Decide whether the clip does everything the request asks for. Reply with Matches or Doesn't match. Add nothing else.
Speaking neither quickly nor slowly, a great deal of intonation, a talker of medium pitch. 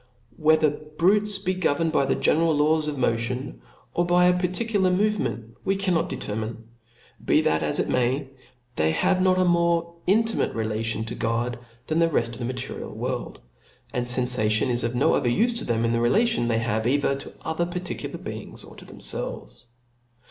Matches